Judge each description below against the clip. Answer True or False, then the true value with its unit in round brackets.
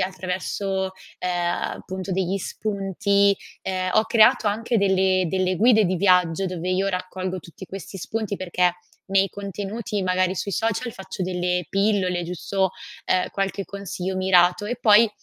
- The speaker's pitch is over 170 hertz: True (190 Hz)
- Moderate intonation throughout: False (1.6 semitones)